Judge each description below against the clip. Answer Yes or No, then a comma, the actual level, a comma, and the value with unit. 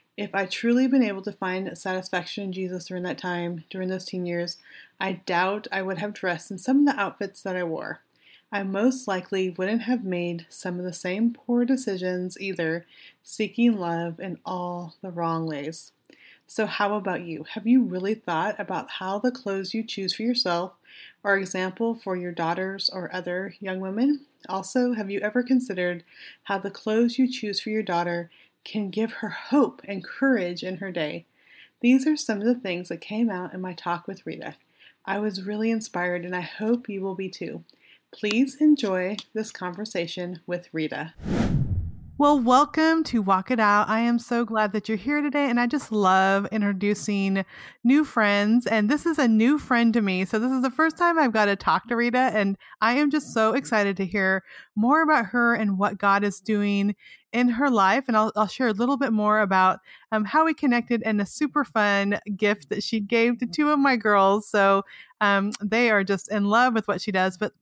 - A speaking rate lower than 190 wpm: No, average, 200 wpm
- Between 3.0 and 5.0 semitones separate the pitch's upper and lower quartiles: Yes, average, 4.1 semitones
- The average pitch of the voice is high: Yes, high, 205 Hz